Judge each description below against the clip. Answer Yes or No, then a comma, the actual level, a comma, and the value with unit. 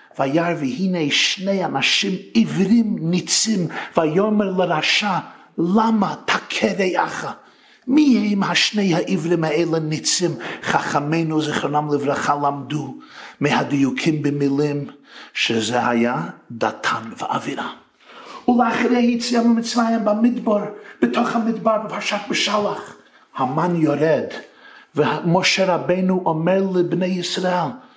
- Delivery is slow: Yes, slow, 90 wpm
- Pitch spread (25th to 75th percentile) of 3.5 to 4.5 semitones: No, wide, 5.6 semitones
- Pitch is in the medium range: Yes, medium, 180 Hz